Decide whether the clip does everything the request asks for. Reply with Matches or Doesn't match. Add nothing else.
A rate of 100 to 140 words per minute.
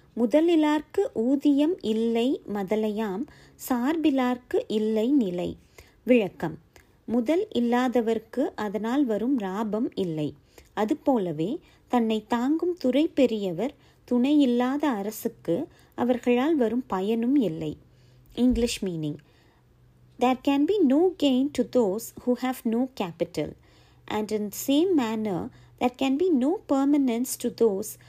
Matches